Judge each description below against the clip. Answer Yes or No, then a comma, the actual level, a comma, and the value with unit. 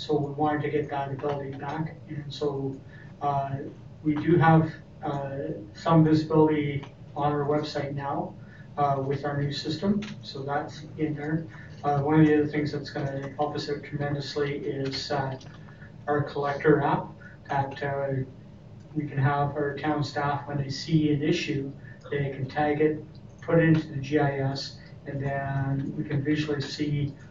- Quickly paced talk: No, average, 165 wpm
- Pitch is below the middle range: No, medium, 145 Hz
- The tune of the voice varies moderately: No, narrow, 1.3 semitones